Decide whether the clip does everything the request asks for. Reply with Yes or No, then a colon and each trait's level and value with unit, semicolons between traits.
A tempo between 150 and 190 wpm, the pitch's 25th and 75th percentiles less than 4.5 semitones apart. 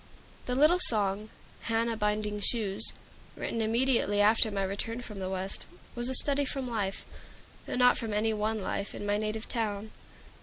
Yes: average, 165 wpm; narrow, 2.4 semitones